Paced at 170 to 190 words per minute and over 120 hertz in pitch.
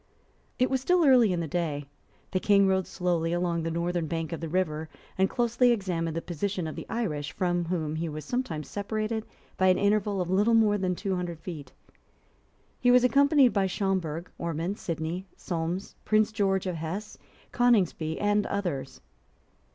Yes: average, 175 wpm; medium, 185 Hz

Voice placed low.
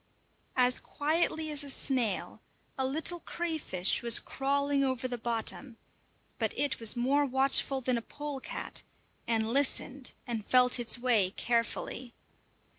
No: very high, 260 Hz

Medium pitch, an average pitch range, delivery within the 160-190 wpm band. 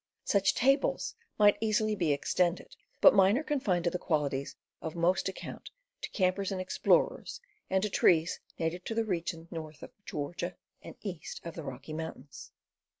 Yes: medium, 180 Hz; average, 3.6 semitones; average, 165 wpm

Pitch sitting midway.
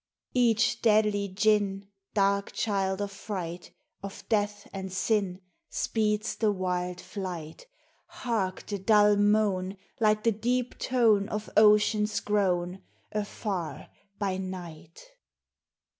No: high, 205 Hz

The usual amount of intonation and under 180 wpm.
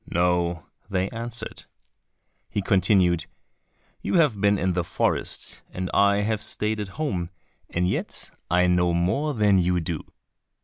Yes: average, 3.1 semitones; average, 140 wpm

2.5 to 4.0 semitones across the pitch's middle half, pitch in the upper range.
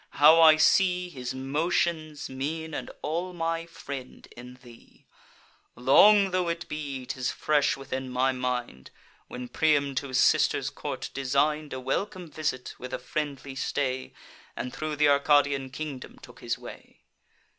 No: average, 3.4 semitones; medium, 145 Hz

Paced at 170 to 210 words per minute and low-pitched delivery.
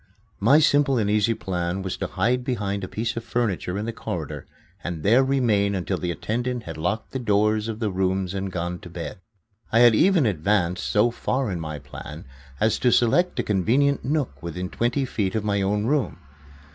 Yes: average, 195 wpm; low, 105 Hz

